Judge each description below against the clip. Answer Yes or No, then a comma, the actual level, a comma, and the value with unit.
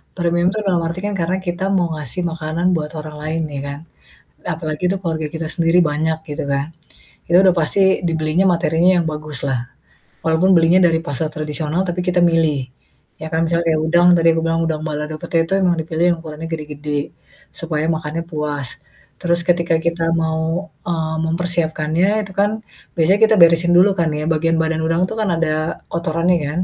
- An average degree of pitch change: No, narrow, 1.9 semitones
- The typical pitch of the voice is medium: Yes, medium, 165 Hz